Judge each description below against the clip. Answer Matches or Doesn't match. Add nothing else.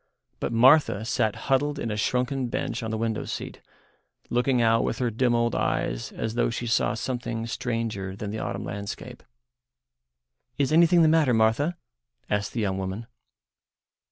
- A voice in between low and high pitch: Doesn't match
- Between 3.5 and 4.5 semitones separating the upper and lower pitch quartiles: Doesn't match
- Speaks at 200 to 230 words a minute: Doesn't match